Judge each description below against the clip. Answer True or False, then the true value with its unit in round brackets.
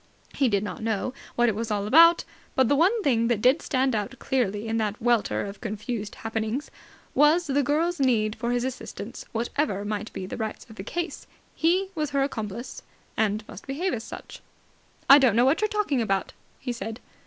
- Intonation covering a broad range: False (4.8 semitones)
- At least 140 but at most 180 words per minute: False (200 wpm)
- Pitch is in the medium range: False (240 Hz)